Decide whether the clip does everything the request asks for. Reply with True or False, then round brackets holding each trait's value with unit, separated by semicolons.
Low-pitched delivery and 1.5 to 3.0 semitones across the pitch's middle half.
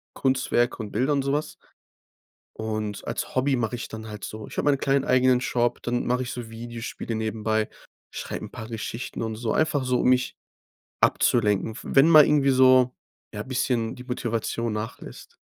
True (120 Hz; 2.7 semitones)